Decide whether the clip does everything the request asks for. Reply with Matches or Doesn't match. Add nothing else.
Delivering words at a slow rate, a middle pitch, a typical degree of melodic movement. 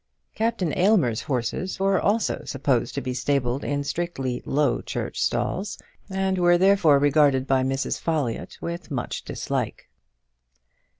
Doesn't match